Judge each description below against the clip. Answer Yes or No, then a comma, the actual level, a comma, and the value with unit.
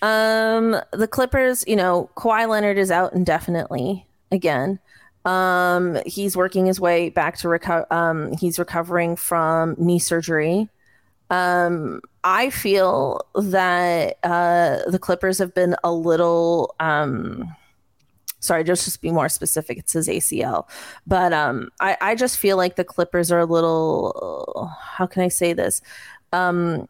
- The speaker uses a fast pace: No, average, 145 wpm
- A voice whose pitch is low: No, medium, 180 Hz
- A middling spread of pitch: No, narrow, 2.3 semitones